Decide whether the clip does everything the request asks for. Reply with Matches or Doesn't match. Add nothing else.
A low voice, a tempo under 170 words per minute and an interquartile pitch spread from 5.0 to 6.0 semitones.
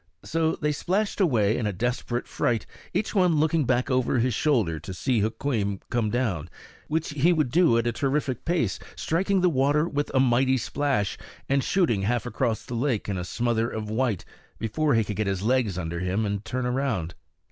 Doesn't match